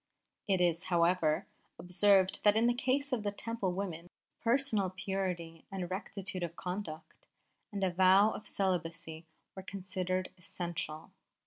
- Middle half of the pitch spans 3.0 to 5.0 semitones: No, narrow, 2.6 semitones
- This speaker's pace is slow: Yes, slow, 130 wpm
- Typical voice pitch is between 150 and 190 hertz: Yes, medium, 185 Hz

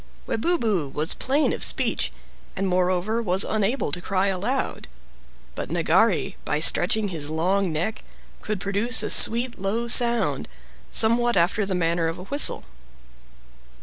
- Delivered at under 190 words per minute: Yes, average, 140 wpm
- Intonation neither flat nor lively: Yes, average, 4.6 semitones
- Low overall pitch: No, high, 200 Hz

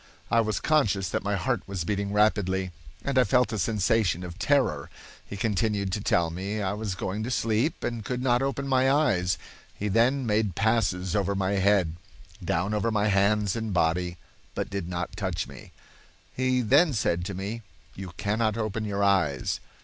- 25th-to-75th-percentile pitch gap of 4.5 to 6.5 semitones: No, average, 3.4 semitones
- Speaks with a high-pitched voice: No, low, 105 Hz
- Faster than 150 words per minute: Yes, average, 180 wpm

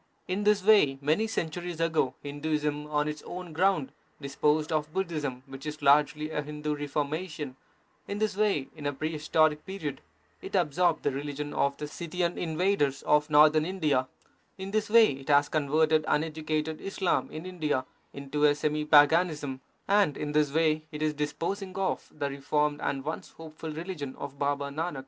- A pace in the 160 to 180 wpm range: Yes, average, 165 wpm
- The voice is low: No, medium, 150 Hz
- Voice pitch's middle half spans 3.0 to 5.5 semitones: No, narrow, 2.5 semitones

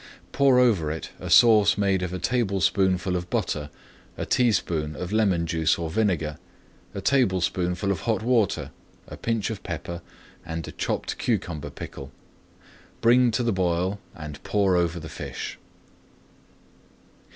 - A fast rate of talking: No, average, 140 wpm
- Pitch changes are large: No, average, 4.7 semitones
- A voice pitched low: Yes, very low, 95 Hz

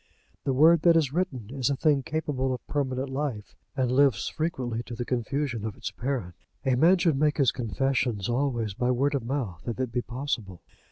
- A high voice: No, low, 130 Hz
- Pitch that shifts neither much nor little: Yes, average, 3.1 semitones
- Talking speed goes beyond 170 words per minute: Yes, average, 200 wpm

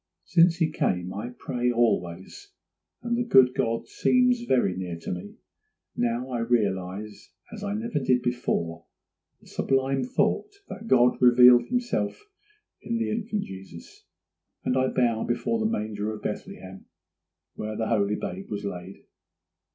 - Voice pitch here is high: No, low, 120 Hz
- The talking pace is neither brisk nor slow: Yes, average, 145 wpm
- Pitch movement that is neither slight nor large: No, wide, 8.9 semitones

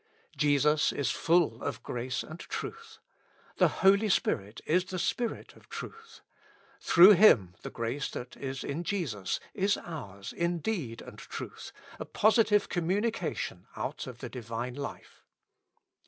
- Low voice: No, medium, 150 Hz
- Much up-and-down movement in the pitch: Yes, wide, 7.9 semitones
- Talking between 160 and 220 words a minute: No, average, 140 wpm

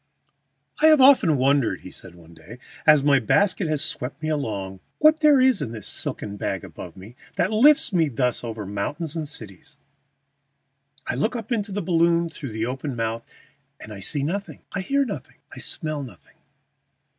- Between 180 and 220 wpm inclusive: Yes, average, 185 wpm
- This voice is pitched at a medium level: Yes, medium, 145 Hz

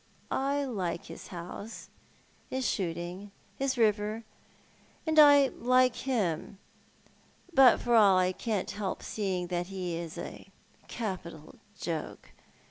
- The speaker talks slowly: Yes, slow, 125 wpm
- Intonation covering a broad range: Yes, wide, 6.0 semitones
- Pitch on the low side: No, high, 205 Hz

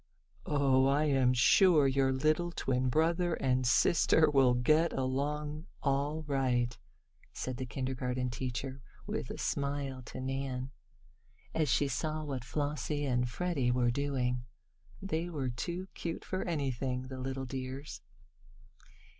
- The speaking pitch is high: No, low, 135 Hz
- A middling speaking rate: No, slow, 130 wpm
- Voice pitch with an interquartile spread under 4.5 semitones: Yes, average, 2.9 semitones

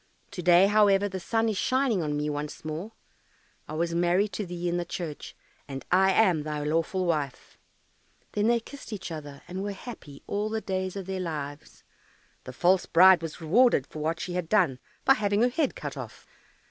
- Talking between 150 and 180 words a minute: No, average, 200 wpm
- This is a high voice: No, medium, 180 Hz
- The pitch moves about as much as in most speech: Yes, average, 4.6 semitones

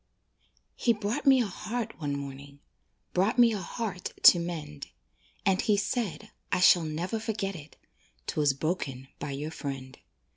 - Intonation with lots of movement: Yes, wide, 6.8 semitones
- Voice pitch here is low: No, medium, 180 Hz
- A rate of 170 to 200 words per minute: No, average, 150 wpm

